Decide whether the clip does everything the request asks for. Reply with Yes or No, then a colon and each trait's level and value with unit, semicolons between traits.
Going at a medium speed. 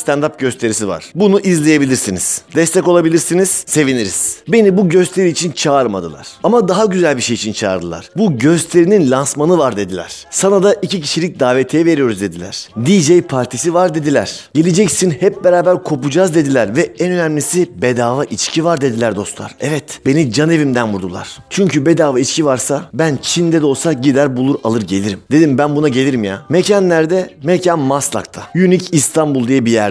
No: fast, 160 wpm